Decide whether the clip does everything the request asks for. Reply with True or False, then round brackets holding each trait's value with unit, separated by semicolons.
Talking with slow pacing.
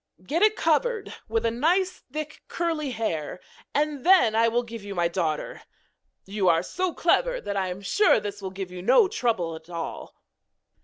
False (175 wpm)